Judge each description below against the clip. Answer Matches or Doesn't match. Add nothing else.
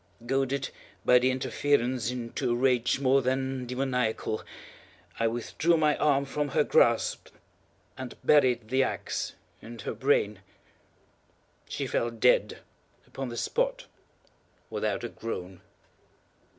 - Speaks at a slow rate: Matches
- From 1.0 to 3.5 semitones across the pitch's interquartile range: Matches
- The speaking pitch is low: Matches